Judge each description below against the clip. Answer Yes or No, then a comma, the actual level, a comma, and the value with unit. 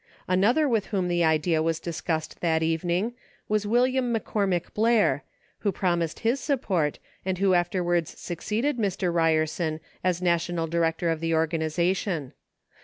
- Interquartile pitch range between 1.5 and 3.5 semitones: No, average, 4.0 semitones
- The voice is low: No, medium, 175 Hz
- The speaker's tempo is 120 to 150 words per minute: Yes, average, 140 wpm